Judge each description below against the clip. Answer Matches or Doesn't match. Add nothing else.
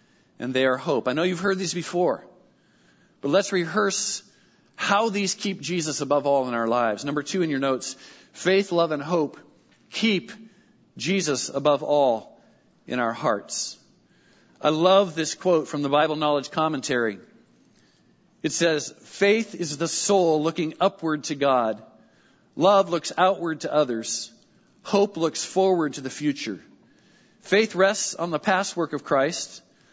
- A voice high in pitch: Doesn't match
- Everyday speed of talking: Matches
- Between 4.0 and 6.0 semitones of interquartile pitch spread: Matches